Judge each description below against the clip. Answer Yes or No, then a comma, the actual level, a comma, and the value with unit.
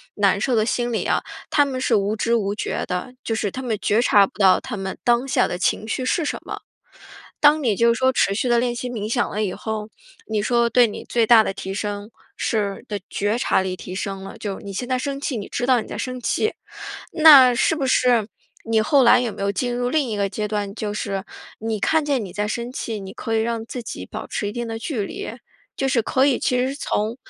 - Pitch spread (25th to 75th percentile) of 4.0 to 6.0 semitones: No, average, 3.4 semitones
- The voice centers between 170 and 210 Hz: No, high, 230 Hz